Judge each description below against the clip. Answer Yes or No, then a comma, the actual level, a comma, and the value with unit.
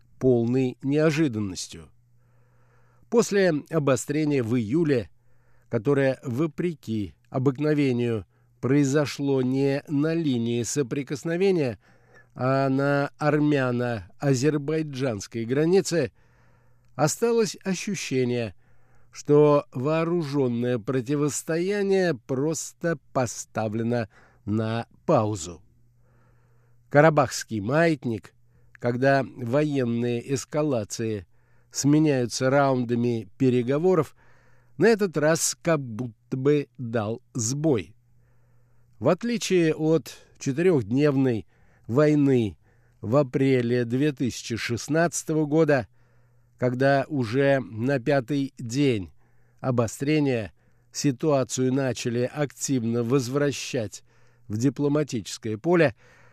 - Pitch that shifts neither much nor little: Yes, average, 3.6 semitones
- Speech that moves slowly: Yes, slow, 70 wpm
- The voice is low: Yes, low, 130 Hz